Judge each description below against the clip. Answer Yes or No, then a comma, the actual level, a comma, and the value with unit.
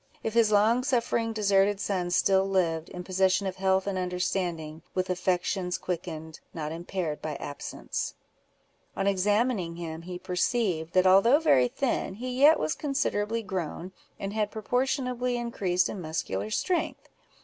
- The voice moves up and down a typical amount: Yes, average, 3.9 semitones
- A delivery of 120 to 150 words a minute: Yes, average, 145 wpm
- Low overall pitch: No, high, 190 Hz